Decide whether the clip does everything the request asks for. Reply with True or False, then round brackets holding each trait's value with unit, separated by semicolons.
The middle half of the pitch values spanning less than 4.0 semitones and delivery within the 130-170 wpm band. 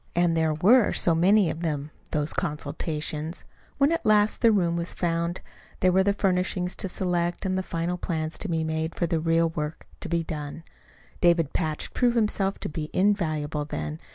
False (3.0 semitones; 185 wpm)